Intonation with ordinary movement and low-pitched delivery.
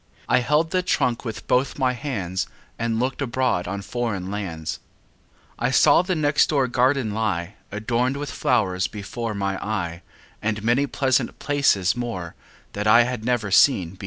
Yes: average, 4.5 semitones; low, 115 Hz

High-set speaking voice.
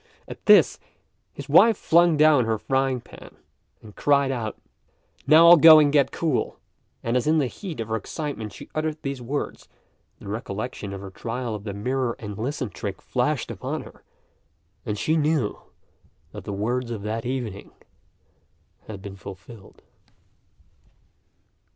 No: low, 125 Hz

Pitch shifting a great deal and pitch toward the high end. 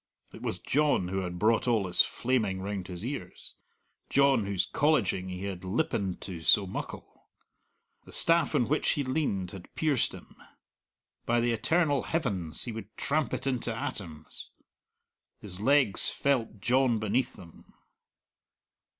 No: wide, 6.2 semitones; low, 115 Hz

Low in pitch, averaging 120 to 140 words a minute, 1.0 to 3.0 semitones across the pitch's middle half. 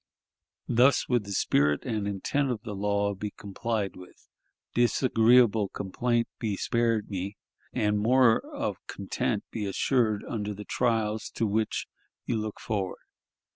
Yes: low, 110 Hz; slow, 135 wpm; average, 2.7 semitones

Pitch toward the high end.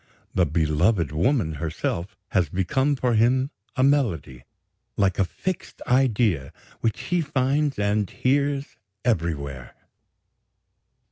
No: low, 105 Hz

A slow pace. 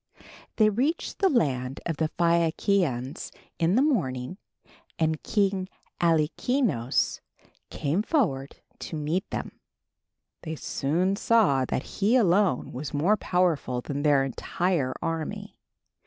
Yes: slow, 115 wpm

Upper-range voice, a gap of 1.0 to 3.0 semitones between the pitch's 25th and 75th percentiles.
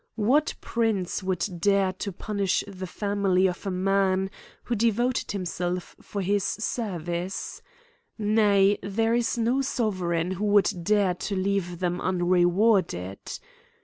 Yes: high, 195 Hz; narrow, 2.6 semitones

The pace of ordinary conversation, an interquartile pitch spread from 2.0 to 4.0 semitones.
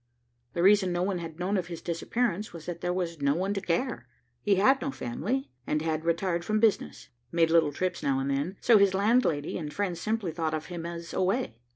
No: fast, 220 wpm; average, 3.6 semitones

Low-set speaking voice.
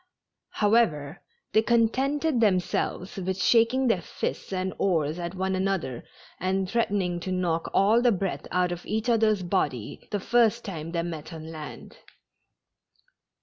No: high, 190 Hz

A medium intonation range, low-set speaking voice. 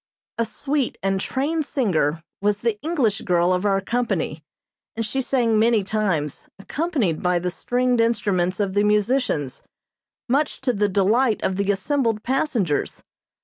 No: average, 4.7 semitones; high, 215 Hz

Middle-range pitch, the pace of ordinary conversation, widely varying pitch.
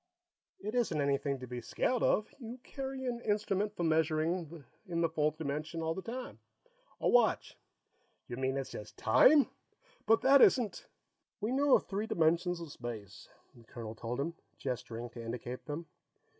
Yes: medium, 160 Hz; average, 170 wpm; wide, 8.3 semitones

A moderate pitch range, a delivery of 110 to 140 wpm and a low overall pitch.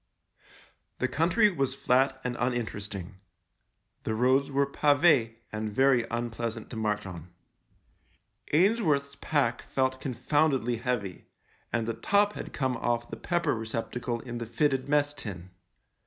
Yes: average, 3.7 semitones; slow, 135 wpm; low, 125 Hz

